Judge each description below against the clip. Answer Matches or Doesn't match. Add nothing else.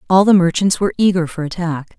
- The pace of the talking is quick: Matches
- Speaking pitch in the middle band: Matches